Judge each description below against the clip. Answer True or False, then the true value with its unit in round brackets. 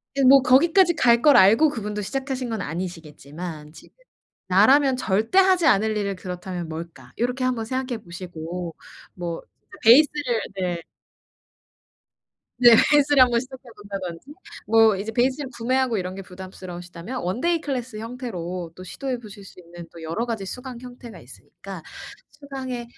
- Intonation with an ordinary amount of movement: False (6.2 semitones)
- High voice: True (225 Hz)